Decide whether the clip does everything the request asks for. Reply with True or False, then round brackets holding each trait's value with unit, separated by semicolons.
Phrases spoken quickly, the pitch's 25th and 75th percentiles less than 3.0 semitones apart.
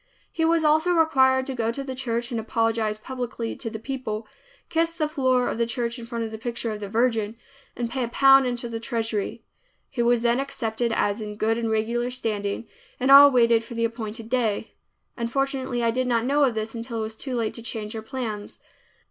True (215 wpm; 2.6 semitones)